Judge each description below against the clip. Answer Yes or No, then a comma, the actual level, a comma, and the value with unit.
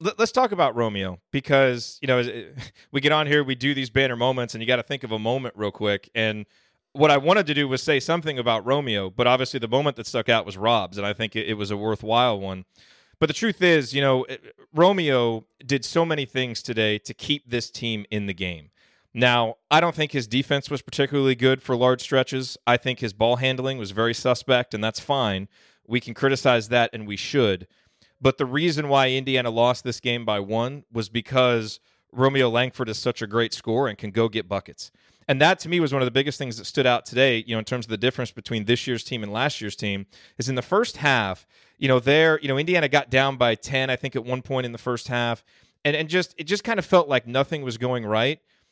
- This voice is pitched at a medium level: No, low, 125 Hz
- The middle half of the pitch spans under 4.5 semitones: Yes, average, 3.4 semitones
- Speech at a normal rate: No, fast, 240 wpm